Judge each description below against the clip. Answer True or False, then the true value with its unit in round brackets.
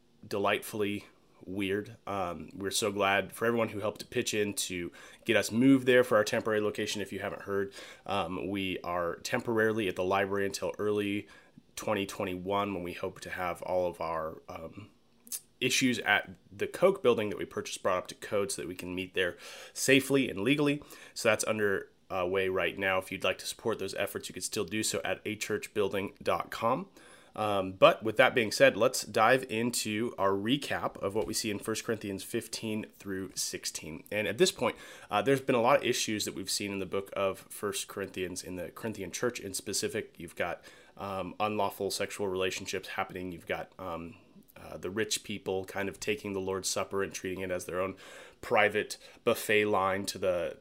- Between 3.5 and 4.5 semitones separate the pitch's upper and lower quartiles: False (2.5 semitones)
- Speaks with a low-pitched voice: True (100 Hz)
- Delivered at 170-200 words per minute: True (195 wpm)